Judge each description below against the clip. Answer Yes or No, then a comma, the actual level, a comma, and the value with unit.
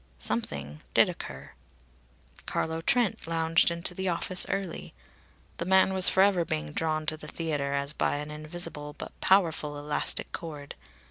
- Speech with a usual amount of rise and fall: Yes, average, 3.2 semitones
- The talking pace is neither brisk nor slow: Yes, average, 145 wpm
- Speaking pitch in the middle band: Yes, medium, 160 Hz